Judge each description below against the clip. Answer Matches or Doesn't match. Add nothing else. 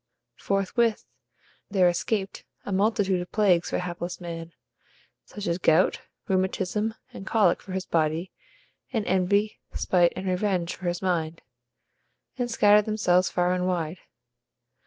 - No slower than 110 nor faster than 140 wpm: Matches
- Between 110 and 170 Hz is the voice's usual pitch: Doesn't match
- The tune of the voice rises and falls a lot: Doesn't match